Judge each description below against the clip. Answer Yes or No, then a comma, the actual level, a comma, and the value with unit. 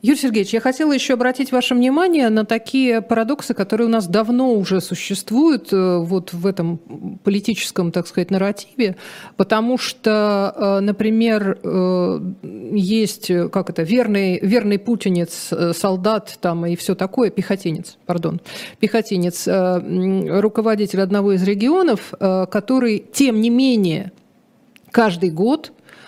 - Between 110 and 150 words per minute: Yes, average, 115 wpm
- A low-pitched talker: No, high, 205 Hz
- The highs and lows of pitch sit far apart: No, average, 3.8 semitones